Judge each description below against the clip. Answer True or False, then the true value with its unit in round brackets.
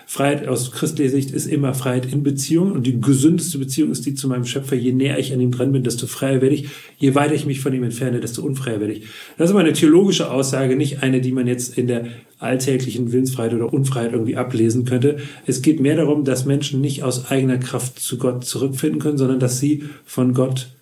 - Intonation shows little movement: True (2.2 semitones)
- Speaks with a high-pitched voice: False (135 Hz)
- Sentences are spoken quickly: True (230 wpm)